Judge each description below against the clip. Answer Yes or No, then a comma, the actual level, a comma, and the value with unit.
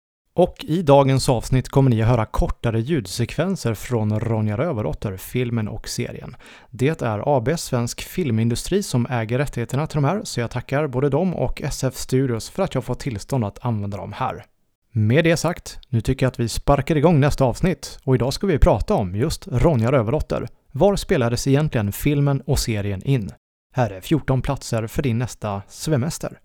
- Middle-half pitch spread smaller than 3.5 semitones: No, average, 4.0 semitones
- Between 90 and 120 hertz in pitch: No, low, 130 Hz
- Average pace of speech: Yes, average, 180 wpm